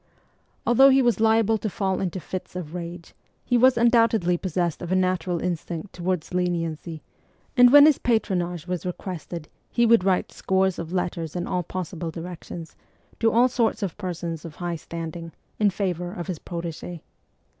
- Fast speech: No, average, 170 wpm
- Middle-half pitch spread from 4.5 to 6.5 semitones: No, average, 3.8 semitones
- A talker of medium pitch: Yes, medium, 180 Hz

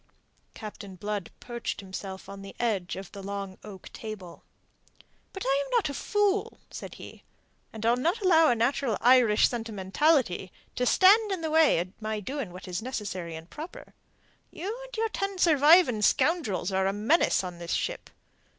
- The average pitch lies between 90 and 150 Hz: No, high, 225 Hz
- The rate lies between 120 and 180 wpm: Yes, average, 170 wpm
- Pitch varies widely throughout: Yes, wide, 8.7 semitones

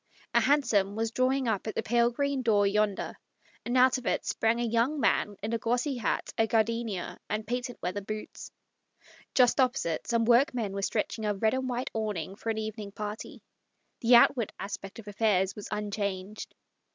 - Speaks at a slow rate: No, average, 185 wpm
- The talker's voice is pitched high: Yes, high, 225 Hz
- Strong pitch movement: No, average, 2.8 semitones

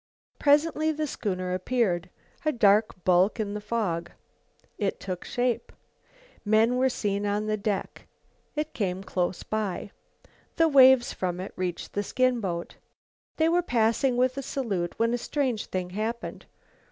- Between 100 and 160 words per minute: Yes, average, 155 wpm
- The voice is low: No, high, 215 Hz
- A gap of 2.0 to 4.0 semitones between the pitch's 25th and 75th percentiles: No, average, 5.2 semitones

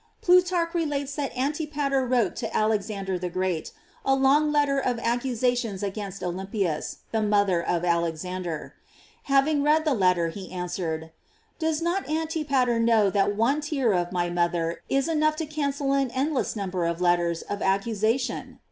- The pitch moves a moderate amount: No, wide, 7.6 semitones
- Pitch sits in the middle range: No, high, 230 Hz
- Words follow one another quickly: No, average, 160 wpm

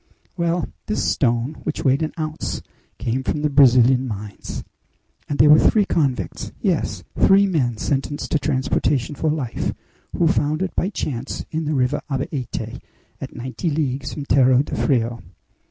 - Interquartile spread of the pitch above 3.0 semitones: Yes, average, 3.5 semitones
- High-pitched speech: No, medium, 140 Hz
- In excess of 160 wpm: No, average, 155 wpm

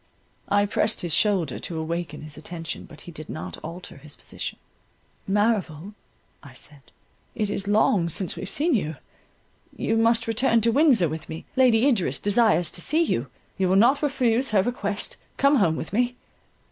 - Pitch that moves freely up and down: Yes, wide, 6.1 semitones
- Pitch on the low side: No, high, 200 Hz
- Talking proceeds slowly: No, average, 165 wpm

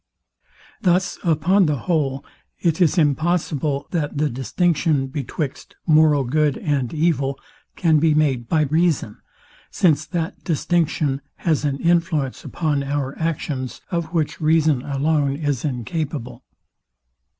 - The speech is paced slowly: Yes, slow, 120 wpm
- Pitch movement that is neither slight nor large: Yes, average, 3.0 semitones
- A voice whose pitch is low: No, medium, 150 Hz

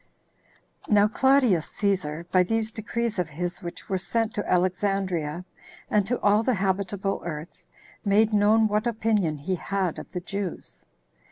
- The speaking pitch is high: Yes, high, 200 Hz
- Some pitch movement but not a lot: Yes, average, 3.3 semitones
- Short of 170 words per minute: Yes, average, 155 wpm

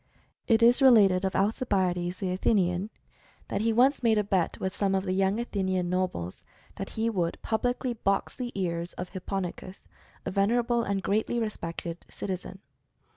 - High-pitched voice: Yes, high, 195 Hz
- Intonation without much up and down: No, average, 3.5 semitones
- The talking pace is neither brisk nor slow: Yes, average, 165 wpm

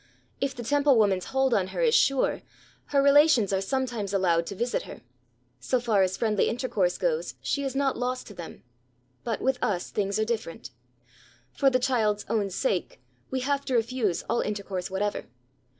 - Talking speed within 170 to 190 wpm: Yes, average, 180 wpm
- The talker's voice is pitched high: Yes, high, 230 Hz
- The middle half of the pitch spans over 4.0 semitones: Yes, average, 5.1 semitones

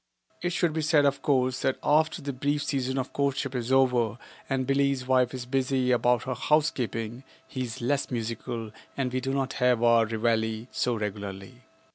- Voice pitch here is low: Yes, low, 130 Hz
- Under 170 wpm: No, average, 180 wpm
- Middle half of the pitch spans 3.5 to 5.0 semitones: No, average, 2.7 semitones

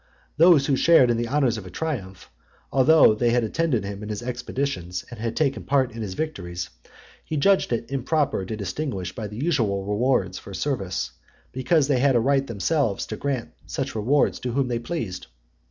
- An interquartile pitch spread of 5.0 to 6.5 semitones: Yes, wide, 5.4 semitones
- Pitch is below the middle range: Yes, low, 120 Hz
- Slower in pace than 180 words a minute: No, average, 185 wpm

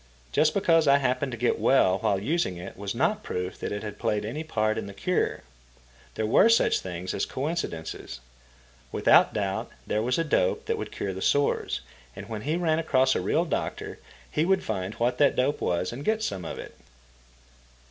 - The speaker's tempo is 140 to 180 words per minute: No, average, 200 wpm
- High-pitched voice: No, low, 125 Hz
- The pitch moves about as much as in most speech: No, wide, 7.5 semitones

